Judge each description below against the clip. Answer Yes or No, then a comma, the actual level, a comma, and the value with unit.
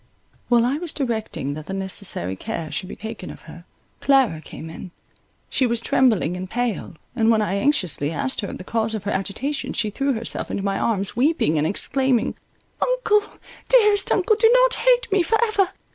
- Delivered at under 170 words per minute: No, average, 185 wpm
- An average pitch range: No, wide, 7.5 semitones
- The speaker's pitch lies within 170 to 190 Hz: No, high, 230 Hz